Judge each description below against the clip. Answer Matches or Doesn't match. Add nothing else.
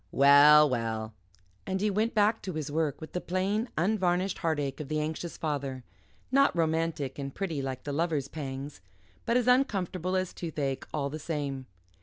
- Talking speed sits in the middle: Matches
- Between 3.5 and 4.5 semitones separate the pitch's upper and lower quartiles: Doesn't match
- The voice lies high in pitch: Doesn't match